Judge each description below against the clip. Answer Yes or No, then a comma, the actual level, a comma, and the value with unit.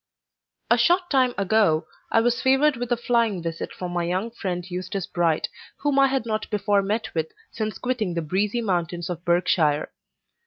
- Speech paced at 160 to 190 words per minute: Yes, average, 180 wpm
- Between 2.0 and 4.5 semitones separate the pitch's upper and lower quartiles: No, average, 5.3 semitones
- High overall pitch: Yes, high, 200 Hz